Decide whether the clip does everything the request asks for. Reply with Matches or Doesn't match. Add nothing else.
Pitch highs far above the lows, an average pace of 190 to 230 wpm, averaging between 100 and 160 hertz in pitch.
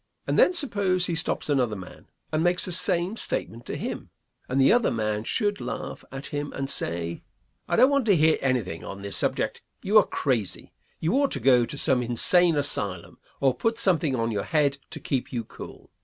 Matches